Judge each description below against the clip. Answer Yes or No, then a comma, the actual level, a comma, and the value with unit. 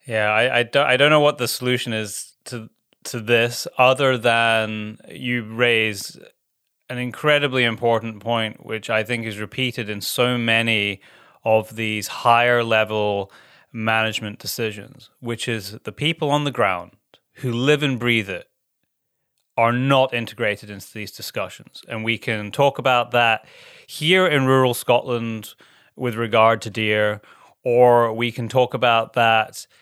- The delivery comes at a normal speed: Yes, average, 150 wpm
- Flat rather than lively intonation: Yes, narrow, 2.2 semitones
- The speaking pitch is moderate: No, low, 115 Hz